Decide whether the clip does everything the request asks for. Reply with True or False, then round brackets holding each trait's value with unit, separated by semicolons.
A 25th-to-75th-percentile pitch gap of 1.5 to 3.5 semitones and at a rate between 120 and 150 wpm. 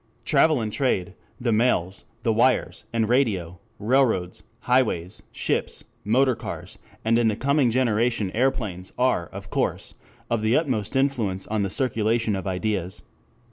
False (4.3 semitones; 140 wpm)